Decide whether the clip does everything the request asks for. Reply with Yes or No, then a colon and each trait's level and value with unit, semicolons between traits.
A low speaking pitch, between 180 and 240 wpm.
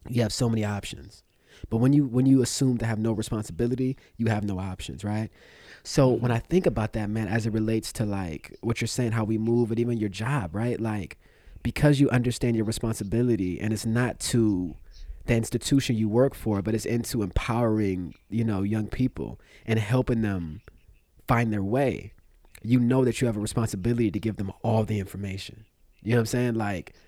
Yes: low, 110 Hz; average, 200 wpm